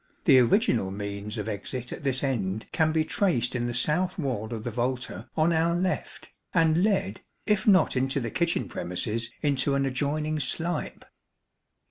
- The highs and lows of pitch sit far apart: Yes, wide, 5.7 semitones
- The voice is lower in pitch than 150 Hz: Yes, low, 135 Hz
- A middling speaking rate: Yes, average, 165 wpm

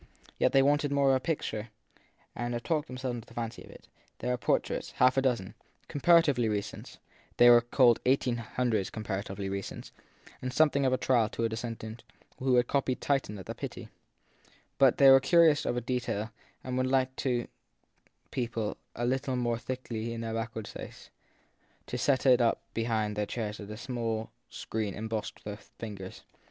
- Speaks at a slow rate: No, average, 175 wpm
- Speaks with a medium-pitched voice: No, low, 120 Hz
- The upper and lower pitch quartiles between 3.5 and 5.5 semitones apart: No, average, 2.8 semitones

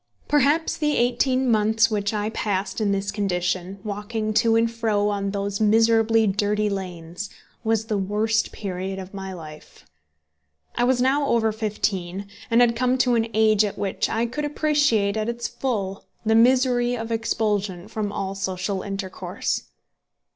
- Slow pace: No, average, 155 wpm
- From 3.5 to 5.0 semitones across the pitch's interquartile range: No, average, 2.8 semitones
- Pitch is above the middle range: Yes, high, 215 Hz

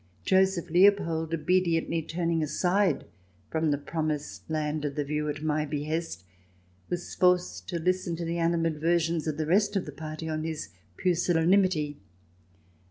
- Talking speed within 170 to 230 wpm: No, average, 145 wpm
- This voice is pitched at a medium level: Yes, medium, 165 Hz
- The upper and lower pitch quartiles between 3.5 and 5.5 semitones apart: No, narrow, 2.5 semitones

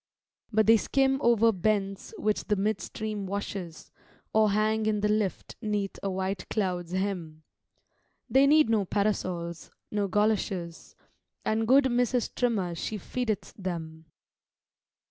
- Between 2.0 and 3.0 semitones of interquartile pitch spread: Yes, average, 2.7 semitones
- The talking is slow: Yes, slow, 125 wpm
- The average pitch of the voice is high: Yes, high, 210 Hz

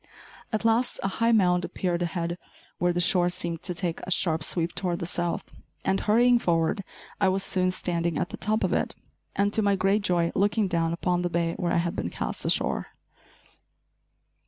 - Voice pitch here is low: No, medium, 180 Hz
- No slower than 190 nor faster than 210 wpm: Yes, average, 195 wpm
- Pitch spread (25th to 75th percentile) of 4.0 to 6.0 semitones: No, narrow, 2.5 semitones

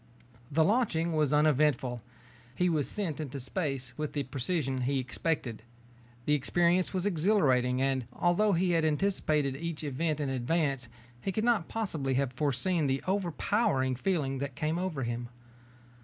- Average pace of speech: Yes, average, 150 wpm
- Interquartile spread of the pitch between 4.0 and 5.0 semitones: Yes, average, 4.7 semitones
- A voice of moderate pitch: Yes, medium, 150 Hz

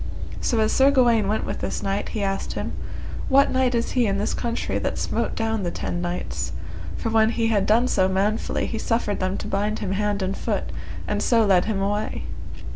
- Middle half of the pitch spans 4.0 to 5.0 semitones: No, average, 2.8 semitones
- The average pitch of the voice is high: Yes, high, 215 Hz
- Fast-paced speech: Yes, fast, 210 wpm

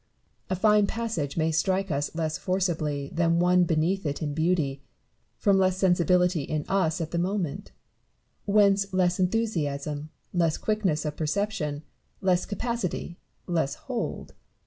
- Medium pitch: Yes, medium, 175 Hz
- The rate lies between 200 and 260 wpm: No, slow, 135 wpm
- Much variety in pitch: No, average, 3.7 semitones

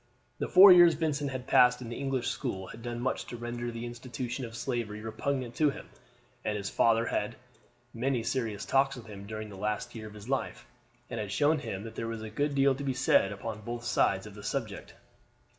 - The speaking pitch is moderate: No, low, 120 Hz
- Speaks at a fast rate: Yes, fast, 225 wpm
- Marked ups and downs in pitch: No, average, 3.6 semitones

